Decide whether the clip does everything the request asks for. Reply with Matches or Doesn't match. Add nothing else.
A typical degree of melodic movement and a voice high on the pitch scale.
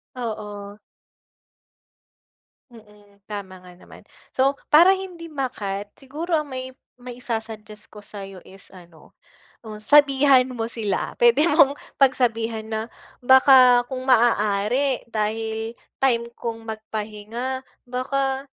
Matches